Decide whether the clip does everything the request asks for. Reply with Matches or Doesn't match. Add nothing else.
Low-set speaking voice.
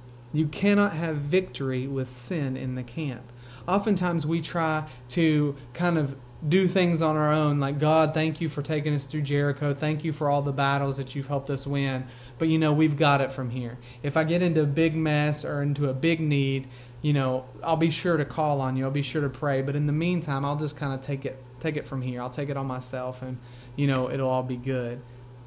Doesn't match